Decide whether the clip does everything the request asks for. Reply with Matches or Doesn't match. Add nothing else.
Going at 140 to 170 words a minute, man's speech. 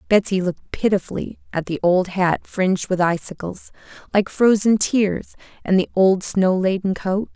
Doesn't match